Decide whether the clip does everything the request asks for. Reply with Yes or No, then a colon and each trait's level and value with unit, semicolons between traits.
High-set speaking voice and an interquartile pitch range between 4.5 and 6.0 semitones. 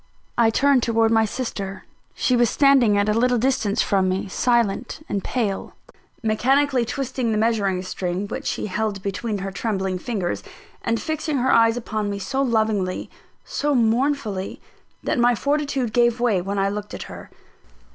No: high, 225 Hz; average, 3.8 semitones